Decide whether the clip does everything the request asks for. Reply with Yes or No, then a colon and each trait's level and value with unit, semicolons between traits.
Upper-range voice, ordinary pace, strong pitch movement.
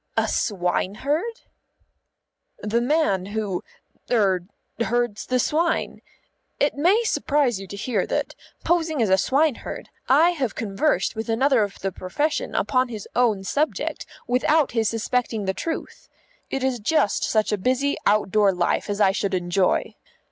Yes: high, 230 Hz; average, 145 wpm; wide, 6.0 semitones